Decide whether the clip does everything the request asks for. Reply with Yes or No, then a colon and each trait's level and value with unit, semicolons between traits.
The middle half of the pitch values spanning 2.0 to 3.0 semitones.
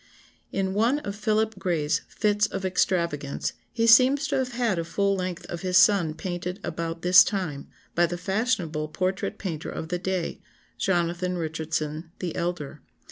No: average, 3.4 semitones